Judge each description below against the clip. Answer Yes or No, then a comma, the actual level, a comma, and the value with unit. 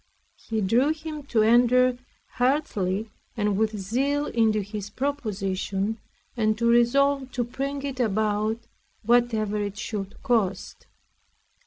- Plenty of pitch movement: No, average, 3.4 semitones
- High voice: Yes, high, 225 Hz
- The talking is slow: Yes, slow, 120 wpm